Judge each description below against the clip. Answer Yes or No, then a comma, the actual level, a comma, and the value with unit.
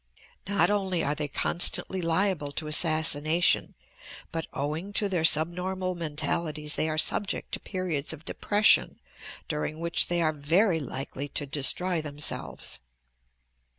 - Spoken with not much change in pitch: No, average, 3.4 semitones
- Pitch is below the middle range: No, medium, 160 Hz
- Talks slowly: Yes, slow, 130 wpm